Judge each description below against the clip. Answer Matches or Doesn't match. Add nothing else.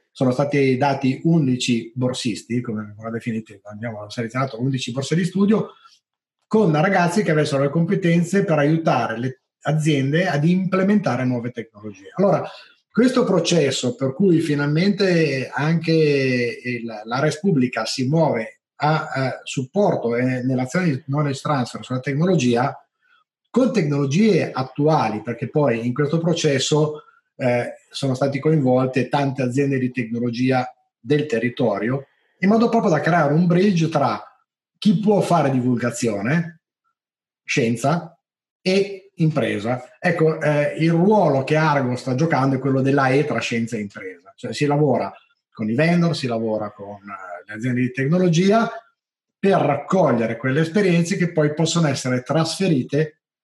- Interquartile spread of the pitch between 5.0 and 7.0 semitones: Matches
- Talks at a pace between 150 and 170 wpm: Doesn't match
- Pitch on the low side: Doesn't match